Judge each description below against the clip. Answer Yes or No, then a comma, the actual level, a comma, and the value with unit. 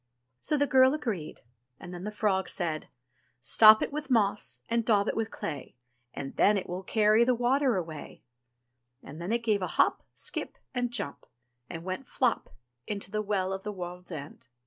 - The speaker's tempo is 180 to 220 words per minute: Yes, average, 185 wpm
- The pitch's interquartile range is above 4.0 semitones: Yes, average, 4.7 semitones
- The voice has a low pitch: No, high, 210 Hz